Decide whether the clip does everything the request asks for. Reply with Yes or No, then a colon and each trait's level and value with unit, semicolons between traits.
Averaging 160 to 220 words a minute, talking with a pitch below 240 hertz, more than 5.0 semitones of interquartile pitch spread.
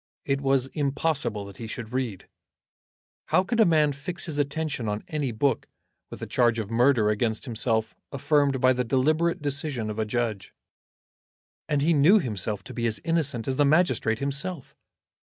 No: average, 170 wpm; low, 135 Hz; average, 4.7 semitones